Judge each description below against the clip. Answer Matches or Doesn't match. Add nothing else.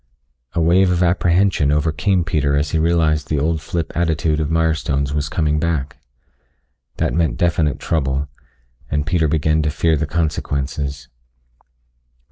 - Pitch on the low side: Matches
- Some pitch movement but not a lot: Doesn't match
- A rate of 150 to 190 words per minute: Doesn't match